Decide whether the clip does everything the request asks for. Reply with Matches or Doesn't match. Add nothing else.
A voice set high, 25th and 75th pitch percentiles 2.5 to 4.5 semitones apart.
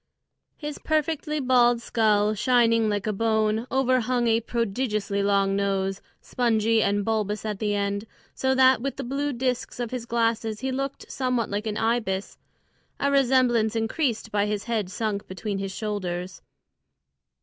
Matches